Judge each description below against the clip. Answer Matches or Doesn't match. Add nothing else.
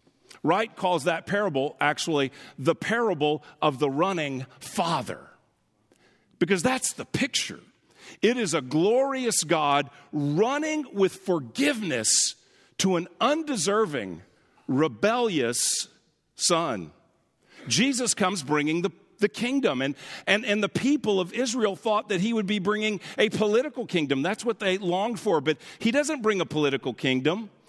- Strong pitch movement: Matches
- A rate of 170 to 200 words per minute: Doesn't match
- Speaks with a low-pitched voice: Doesn't match